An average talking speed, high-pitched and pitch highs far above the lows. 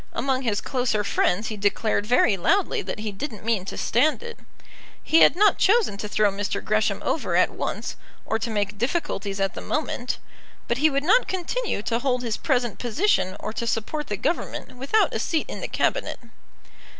Yes: average, 190 wpm; high, 235 Hz; wide, 6.6 semitones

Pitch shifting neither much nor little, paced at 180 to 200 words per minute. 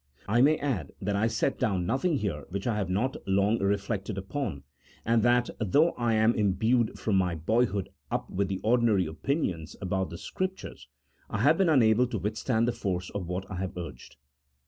Yes: average, 4.2 semitones; average, 190 wpm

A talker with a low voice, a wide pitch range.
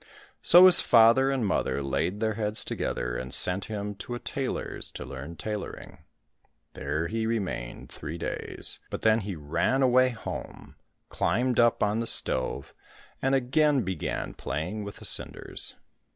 Yes: low, 110 Hz; wide, 6.5 semitones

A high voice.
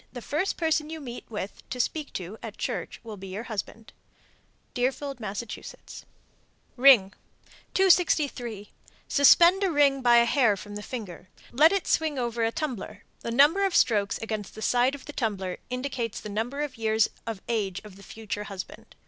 Yes: high, 235 Hz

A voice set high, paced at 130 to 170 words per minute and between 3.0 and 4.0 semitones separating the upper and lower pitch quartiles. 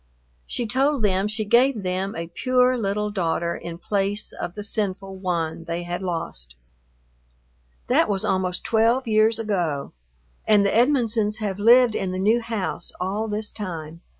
Yes: high, 205 Hz; average, 155 wpm; average, 3.6 semitones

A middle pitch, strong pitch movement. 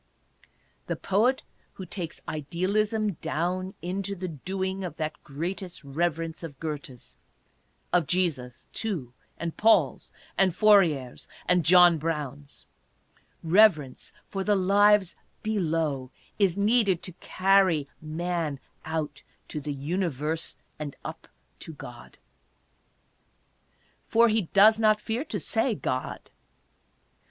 No: medium, 175 Hz; average, 4.4 semitones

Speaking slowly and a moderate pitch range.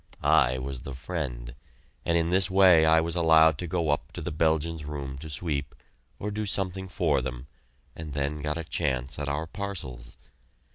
No: average, 185 wpm; average, 3.6 semitones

